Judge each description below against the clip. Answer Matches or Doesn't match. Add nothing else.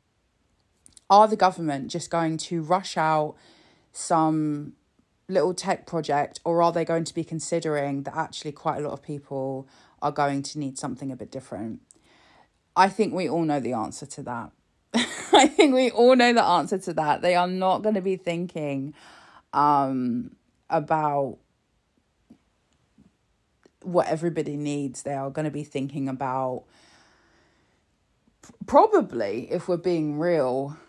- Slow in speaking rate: Doesn't match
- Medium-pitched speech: Matches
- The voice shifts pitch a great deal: Doesn't match